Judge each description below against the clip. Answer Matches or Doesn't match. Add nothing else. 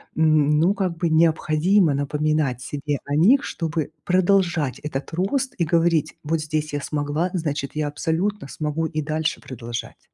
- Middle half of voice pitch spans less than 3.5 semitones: Matches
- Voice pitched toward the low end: Doesn't match